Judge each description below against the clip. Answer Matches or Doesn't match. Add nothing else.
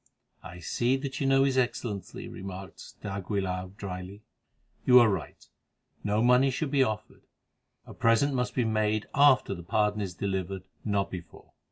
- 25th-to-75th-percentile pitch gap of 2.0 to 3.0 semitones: Doesn't match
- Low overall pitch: Matches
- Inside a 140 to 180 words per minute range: Matches